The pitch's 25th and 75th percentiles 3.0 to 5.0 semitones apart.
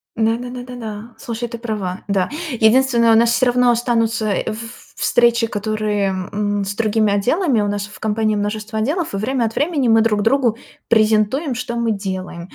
No: narrow, 2.5 semitones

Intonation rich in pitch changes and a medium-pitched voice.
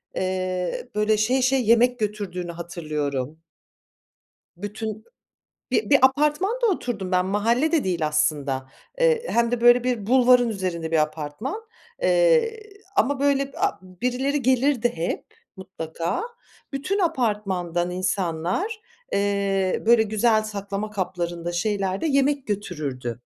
No: wide, 6.8 semitones; high, 210 Hz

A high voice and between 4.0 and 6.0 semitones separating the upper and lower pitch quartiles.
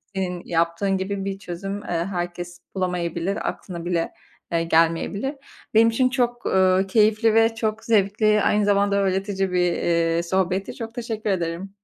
No: high, 195 Hz; average, 3.3 semitones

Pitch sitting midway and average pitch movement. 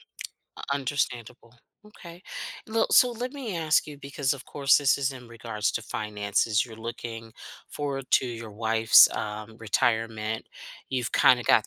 No: low, 120 Hz; average, 4.1 semitones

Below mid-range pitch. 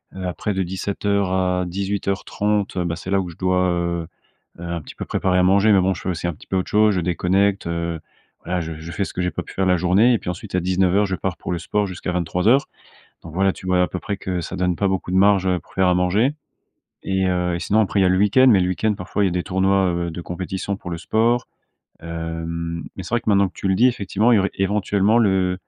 Yes: very low, 95 Hz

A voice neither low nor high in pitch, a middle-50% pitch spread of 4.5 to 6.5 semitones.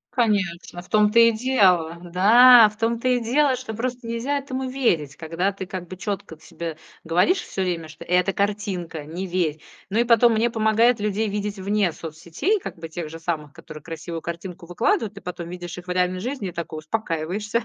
No: high, 195 Hz; average, 5.3 semitones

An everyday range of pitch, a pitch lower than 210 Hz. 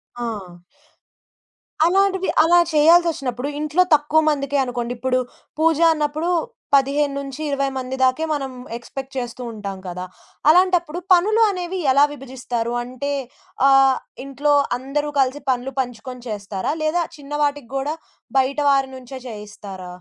No: average, 3.5 semitones; very high, 275 Hz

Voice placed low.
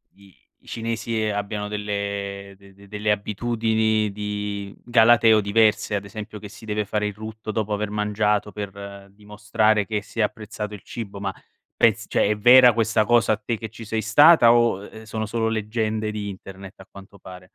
Yes: low, 105 Hz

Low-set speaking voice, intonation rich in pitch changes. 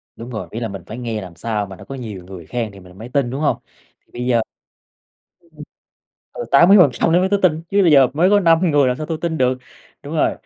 Yes: low, 125 Hz; wide, 6.7 semitones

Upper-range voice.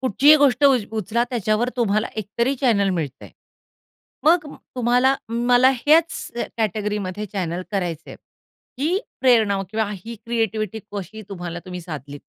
Yes: high, 220 Hz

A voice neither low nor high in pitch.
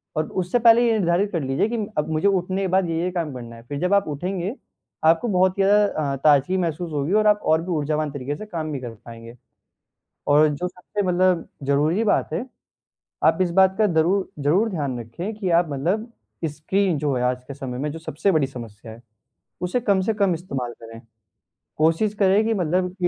Yes: medium, 170 Hz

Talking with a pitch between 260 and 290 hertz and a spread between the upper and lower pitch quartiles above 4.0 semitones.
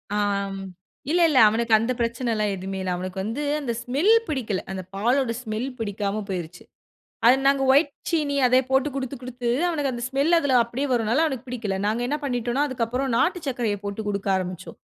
No: high, 240 Hz; average, 4.5 semitones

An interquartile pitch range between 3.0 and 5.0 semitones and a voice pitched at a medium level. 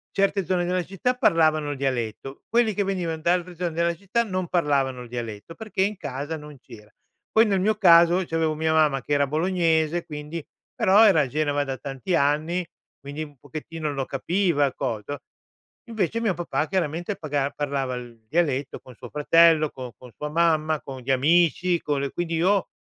Yes: average, 4.0 semitones; medium, 160 Hz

